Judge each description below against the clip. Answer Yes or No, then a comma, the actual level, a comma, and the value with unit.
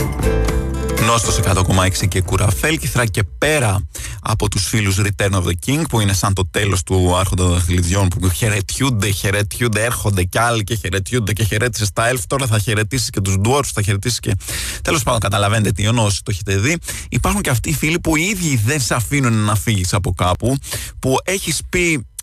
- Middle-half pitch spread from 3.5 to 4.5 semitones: Yes, average, 4.0 semitones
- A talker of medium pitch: No, low, 105 Hz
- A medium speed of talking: No, fast, 190 wpm